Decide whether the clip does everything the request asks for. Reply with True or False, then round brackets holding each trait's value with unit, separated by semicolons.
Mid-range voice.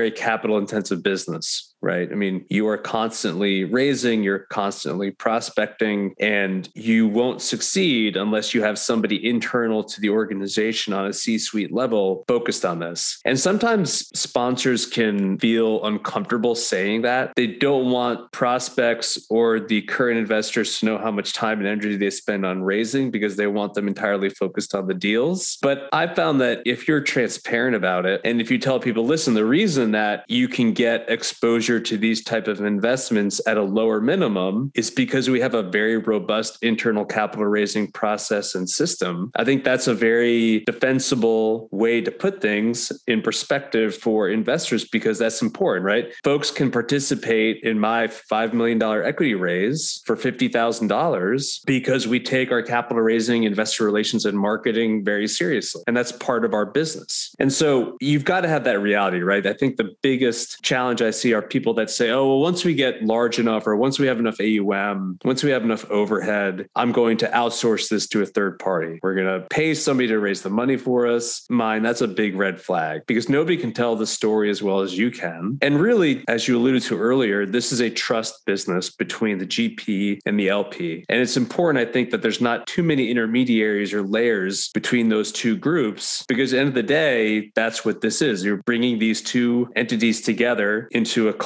False (115 Hz)